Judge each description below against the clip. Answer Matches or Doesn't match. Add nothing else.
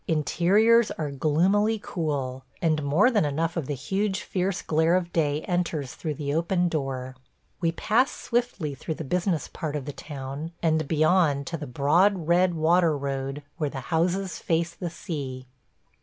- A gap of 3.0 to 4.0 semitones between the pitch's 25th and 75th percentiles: Matches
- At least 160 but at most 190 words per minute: Matches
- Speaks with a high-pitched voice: Doesn't match